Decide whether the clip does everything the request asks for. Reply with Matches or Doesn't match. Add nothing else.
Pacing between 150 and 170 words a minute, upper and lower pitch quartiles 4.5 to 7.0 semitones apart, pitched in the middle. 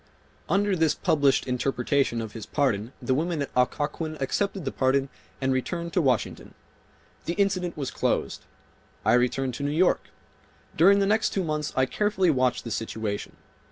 Matches